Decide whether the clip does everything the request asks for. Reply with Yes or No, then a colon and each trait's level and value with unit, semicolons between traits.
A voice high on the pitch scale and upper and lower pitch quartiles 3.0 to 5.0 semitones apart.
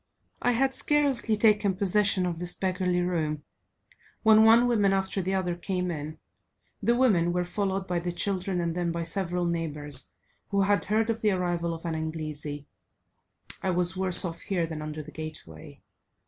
No: medium, 180 Hz; average, 3.4 semitones